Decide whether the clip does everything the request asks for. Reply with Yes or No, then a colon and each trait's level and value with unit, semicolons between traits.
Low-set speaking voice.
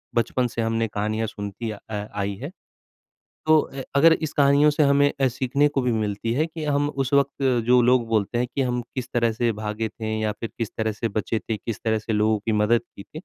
Yes: low, 120 Hz